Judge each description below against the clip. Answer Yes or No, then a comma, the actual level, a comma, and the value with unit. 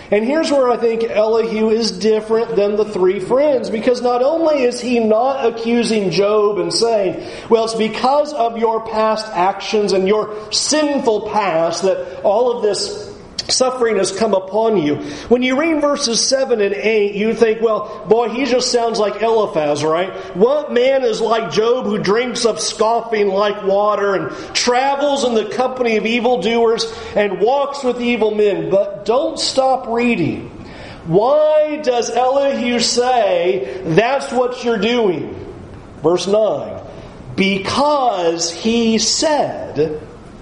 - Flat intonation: No, average, 3.1 semitones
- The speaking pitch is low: No, high, 225 Hz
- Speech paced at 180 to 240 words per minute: No, average, 145 wpm